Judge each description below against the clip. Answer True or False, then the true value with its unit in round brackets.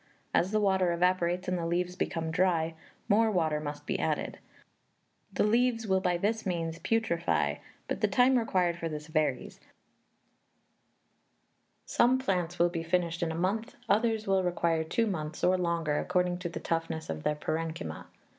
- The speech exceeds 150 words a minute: True (165 wpm)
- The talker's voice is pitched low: False (175 Hz)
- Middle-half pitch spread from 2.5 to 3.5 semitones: True (3.0 semitones)